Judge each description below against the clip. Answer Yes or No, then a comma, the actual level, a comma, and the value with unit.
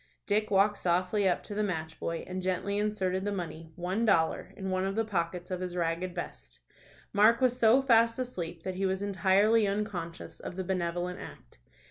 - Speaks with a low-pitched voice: No, high, 190 Hz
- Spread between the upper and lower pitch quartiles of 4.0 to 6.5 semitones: No, average, 3.1 semitones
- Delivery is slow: No, average, 190 wpm